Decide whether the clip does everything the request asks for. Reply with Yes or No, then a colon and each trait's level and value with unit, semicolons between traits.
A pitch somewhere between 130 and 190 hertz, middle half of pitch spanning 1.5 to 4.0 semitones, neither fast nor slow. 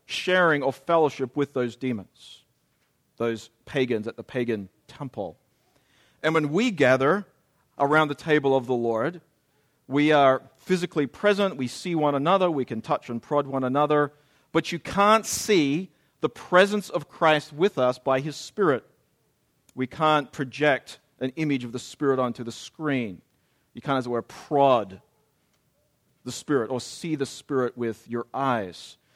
Yes: medium, 140 Hz; average, 3.5 semitones; average, 155 wpm